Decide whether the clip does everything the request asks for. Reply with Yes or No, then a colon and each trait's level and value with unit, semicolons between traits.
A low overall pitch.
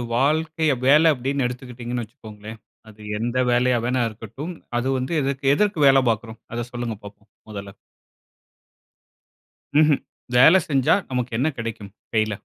Yes: low, 125 Hz